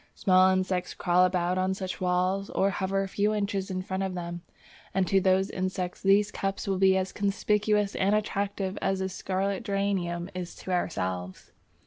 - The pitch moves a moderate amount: No, narrow, 1.3 semitones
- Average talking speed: Yes, average, 175 wpm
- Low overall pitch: No, high, 190 Hz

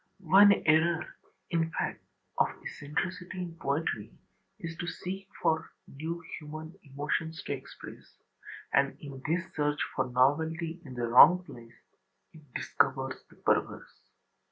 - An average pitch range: Yes, average, 3.6 semitones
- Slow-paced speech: Yes, slow, 130 wpm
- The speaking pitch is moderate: Yes, medium, 160 Hz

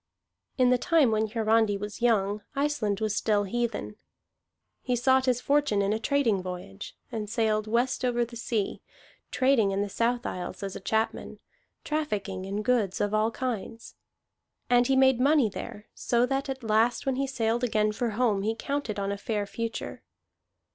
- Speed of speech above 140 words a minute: Yes, average, 175 wpm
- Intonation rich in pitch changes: No, average, 3.3 semitones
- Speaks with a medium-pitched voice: No, high, 225 Hz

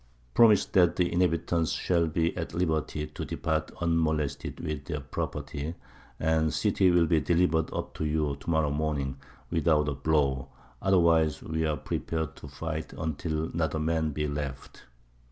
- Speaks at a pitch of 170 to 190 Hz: No, very low, 80 Hz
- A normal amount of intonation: No, narrow, 1.8 semitones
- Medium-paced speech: Yes, average, 160 wpm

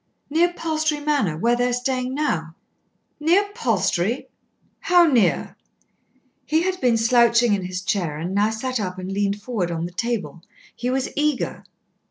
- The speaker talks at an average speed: Yes, average, 160 wpm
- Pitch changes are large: Yes, wide, 7.3 semitones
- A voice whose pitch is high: Yes, high, 235 Hz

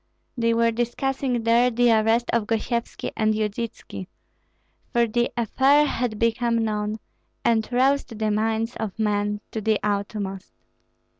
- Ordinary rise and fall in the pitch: No, narrow, 1.9 semitones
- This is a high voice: Yes, high, 225 Hz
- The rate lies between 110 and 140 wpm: Yes, slow, 135 wpm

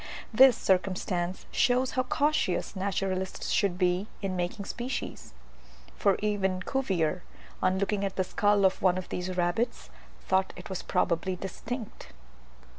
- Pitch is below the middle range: No, high, 190 Hz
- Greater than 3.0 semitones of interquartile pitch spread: No, narrow, 2.4 semitones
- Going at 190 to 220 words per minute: No, slow, 135 wpm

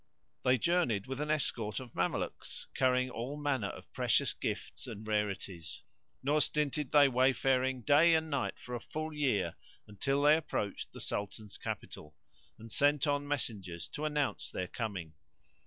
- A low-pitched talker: Yes, low, 130 Hz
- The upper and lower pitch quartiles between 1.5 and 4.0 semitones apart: No, wide, 5.5 semitones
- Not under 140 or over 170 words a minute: Yes, average, 155 wpm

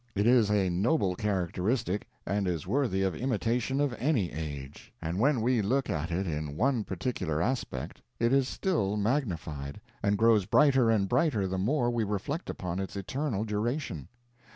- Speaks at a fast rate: No, average, 165 wpm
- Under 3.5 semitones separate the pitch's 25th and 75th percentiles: No, wide, 5.4 semitones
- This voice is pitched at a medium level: No, low, 105 Hz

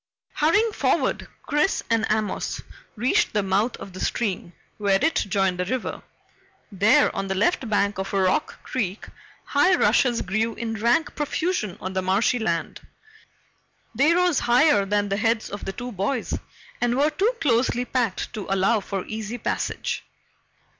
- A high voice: Yes, high, 220 Hz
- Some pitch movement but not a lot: Yes, average, 4.7 semitones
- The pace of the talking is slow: No, average, 155 wpm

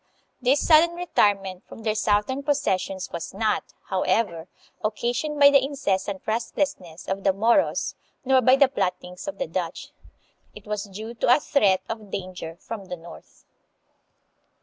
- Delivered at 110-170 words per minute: Yes, average, 150 wpm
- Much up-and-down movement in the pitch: Yes, wide, 5.9 semitones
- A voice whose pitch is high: Yes, high, 215 Hz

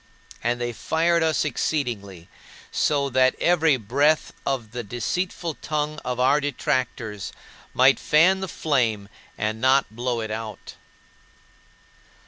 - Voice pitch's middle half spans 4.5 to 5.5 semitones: Yes, average, 5.0 semitones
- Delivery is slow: Yes, slow, 120 wpm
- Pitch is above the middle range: No, low, 130 Hz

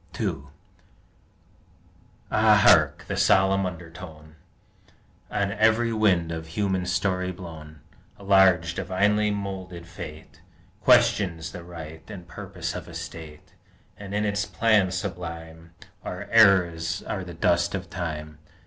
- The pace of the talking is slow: Yes, slow, 125 wpm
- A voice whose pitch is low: Yes, very low, 90 Hz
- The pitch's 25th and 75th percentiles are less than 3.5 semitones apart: Yes, average, 3.0 semitones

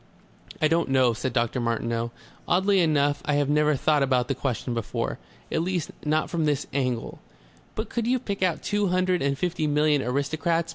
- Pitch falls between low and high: Yes, medium, 150 Hz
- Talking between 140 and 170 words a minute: No, average, 185 wpm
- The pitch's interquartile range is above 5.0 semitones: No, average, 4.7 semitones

